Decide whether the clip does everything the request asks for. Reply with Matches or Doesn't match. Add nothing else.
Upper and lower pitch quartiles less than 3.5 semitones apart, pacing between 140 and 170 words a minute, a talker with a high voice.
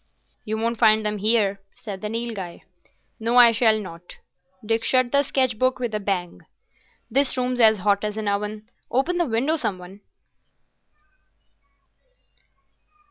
Matches